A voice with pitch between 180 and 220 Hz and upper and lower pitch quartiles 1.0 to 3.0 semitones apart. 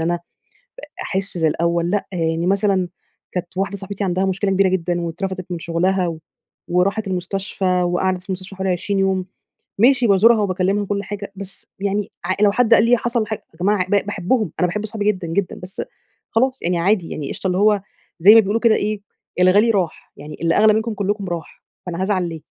Yes: high, 190 Hz; narrow, 2.4 semitones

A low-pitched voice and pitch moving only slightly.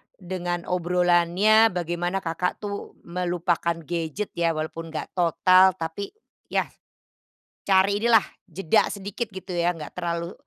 No: medium, 180 Hz; narrow, 2.1 semitones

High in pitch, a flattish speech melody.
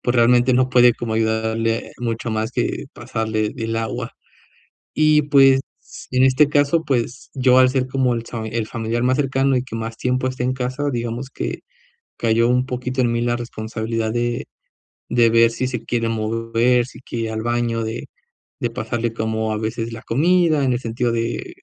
No: low, 120 Hz; narrow, 2.1 semitones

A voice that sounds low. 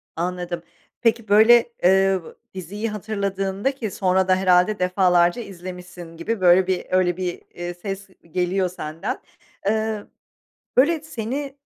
No: high, 190 Hz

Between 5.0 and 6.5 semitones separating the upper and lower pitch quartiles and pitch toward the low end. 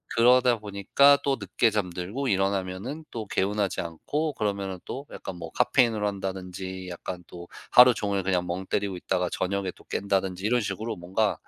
No: average, 3.8 semitones; low, 100 Hz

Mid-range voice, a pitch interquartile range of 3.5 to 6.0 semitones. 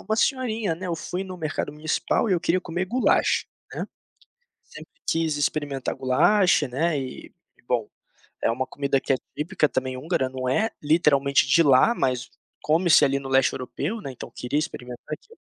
Yes: medium, 150 Hz; average, 4.9 semitones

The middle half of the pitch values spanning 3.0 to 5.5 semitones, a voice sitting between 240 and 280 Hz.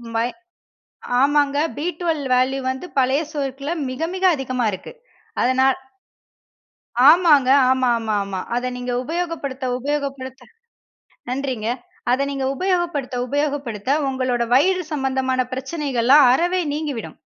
No: narrow, 2.6 semitones; very high, 270 Hz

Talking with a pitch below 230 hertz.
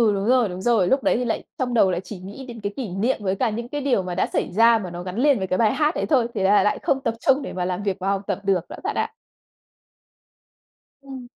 Yes: high, 215 Hz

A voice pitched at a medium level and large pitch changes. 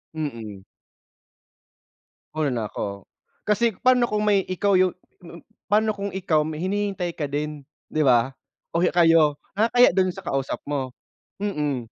Yes: medium, 170 Hz; wide, 5.8 semitones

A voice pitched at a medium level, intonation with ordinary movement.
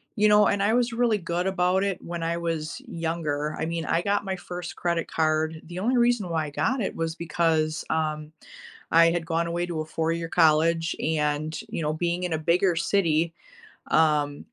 No: medium, 165 Hz; narrow, 2.2 semitones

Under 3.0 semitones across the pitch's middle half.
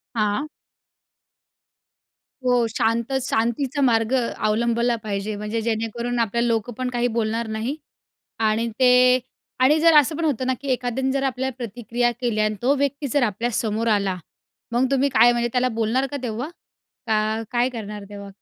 Yes: narrow, 2.6 semitones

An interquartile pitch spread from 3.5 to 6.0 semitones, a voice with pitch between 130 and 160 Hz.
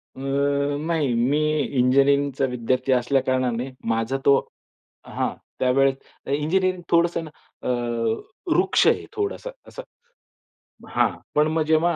Yes: average, 3.9 semitones; medium, 140 Hz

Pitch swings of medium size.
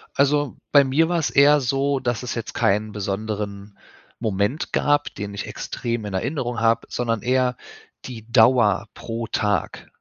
Yes: average, 4.4 semitones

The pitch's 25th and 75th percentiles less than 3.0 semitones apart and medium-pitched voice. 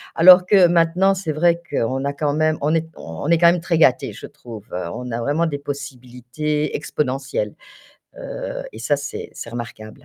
No: average, 4.3 semitones; medium, 150 Hz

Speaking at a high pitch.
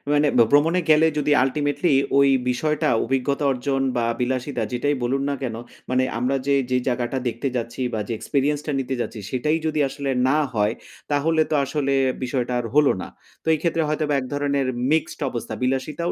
No: medium, 140 Hz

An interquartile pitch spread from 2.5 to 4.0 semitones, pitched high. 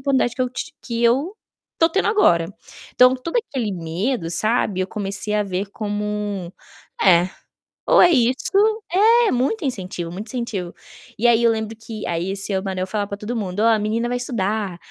No: average, 4.4 semitones; high, 215 Hz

